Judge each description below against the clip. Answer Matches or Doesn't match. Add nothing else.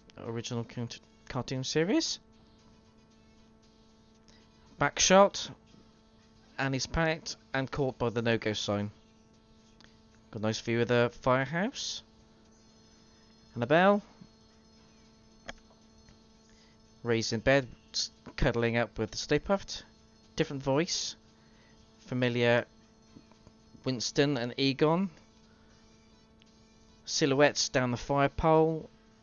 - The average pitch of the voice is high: Doesn't match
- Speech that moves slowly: Matches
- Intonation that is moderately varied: Matches